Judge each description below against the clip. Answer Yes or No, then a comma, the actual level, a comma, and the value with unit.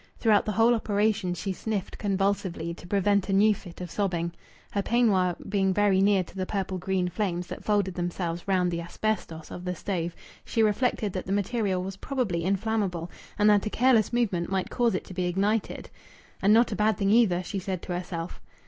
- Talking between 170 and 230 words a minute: Yes, average, 200 wpm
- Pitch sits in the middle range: No, high, 195 Hz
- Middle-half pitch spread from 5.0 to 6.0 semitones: No, average, 2.7 semitones